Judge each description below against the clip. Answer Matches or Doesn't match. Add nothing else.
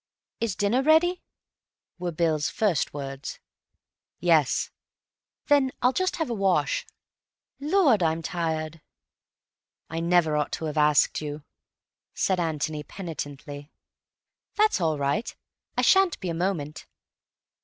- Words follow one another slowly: Matches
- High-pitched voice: Doesn't match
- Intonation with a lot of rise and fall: Matches